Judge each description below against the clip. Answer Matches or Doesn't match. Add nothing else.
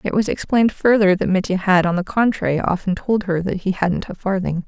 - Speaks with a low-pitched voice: Doesn't match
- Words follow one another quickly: Matches